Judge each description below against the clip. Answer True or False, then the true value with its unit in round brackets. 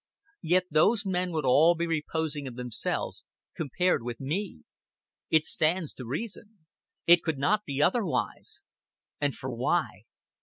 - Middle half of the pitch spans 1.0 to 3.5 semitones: False (4.7 semitones)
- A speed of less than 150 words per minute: True (140 wpm)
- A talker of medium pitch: True (160 Hz)